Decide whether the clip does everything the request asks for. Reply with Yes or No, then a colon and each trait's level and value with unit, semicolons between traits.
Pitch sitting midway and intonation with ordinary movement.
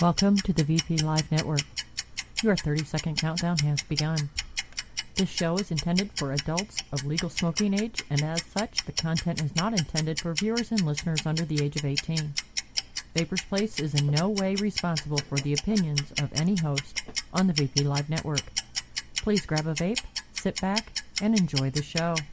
Yes: medium, 160 Hz; average, 4.1 semitones